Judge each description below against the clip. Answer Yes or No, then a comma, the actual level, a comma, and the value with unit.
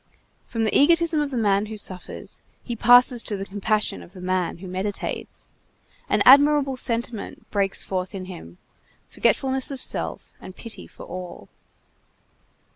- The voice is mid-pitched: No, high, 215 Hz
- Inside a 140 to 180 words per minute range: Yes, average, 150 wpm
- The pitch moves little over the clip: No, average, 5.3 semitones